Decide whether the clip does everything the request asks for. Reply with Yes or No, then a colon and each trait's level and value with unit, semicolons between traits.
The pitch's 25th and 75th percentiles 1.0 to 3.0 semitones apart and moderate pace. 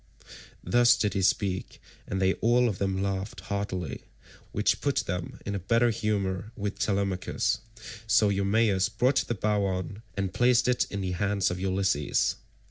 Yes: narrow, 2.4 semitones; average, 160 wpm